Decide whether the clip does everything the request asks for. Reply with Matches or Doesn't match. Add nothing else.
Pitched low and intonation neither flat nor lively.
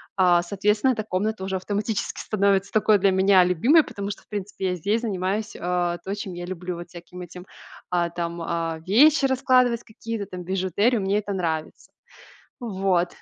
Doesn't match